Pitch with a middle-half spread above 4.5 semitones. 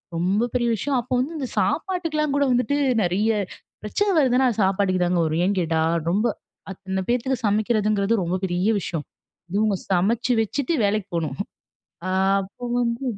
Yes: average, 5.0 semitones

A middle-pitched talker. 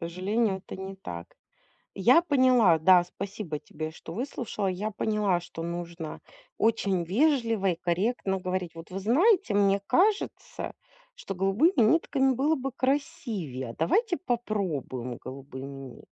No: high, 195 Hz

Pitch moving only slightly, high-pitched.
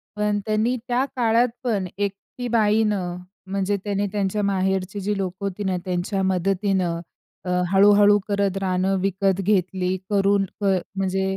Yes: narrow, 1.5 semitones; high, 195 Hz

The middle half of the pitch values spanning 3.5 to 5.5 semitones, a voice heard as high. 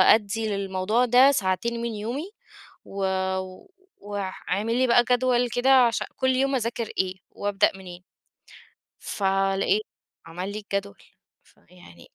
Yes: average, 3.9 semitones; high, 210 Hz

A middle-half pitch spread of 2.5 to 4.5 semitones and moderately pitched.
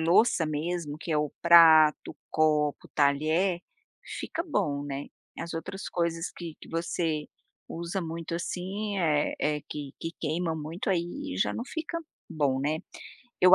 Yes: average, 2.8 semitones; medium, 165 Hz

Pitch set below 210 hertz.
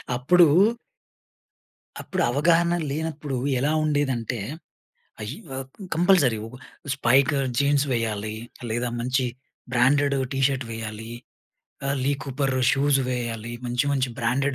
Yes: low, 135 Hz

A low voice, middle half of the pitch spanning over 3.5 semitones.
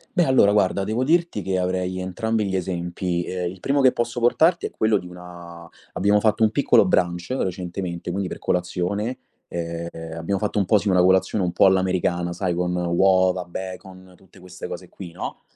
No: very low, 95 Hz; narrow, 2.6 semitones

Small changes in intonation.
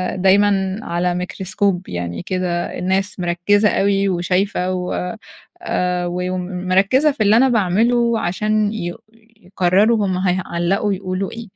Yes: narrow, 2.3 semitones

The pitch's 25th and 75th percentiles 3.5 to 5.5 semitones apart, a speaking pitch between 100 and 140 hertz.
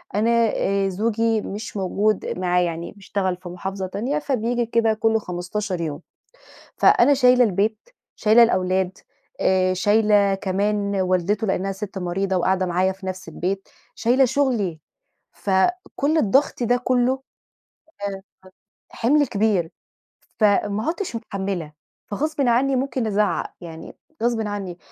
No: average, 3.8 semitones; high, 205 Hz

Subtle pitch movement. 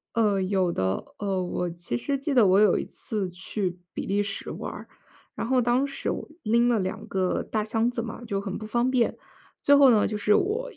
No: average, 4.1 semitones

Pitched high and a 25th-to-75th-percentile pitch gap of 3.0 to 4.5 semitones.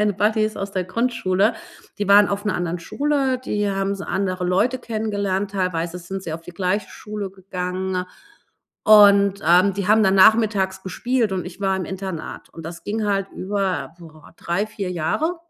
No: high, 195 Hz; narrow, 2.4 semitones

